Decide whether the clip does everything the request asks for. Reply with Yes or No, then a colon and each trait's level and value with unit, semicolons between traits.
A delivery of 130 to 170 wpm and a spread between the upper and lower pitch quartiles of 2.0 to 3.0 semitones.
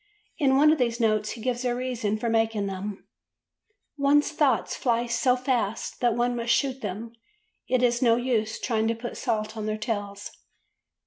No: average, 180 wpm; narrow, 2.6 semitones